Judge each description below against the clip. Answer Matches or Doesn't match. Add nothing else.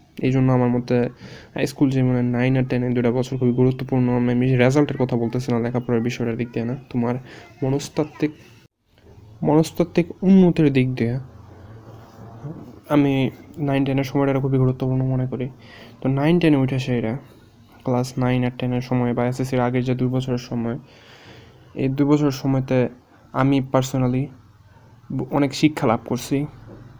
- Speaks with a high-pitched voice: Doesn't match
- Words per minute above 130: Matches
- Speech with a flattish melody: Matches